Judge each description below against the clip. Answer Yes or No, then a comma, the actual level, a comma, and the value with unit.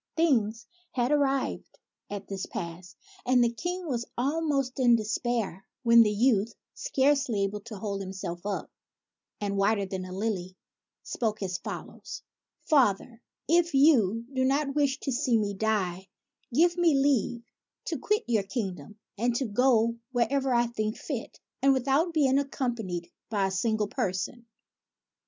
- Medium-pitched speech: No, high, 235 Hz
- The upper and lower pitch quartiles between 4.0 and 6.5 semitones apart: Yes, average, 5.1 semitones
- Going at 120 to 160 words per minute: Yes, average, 155 wpm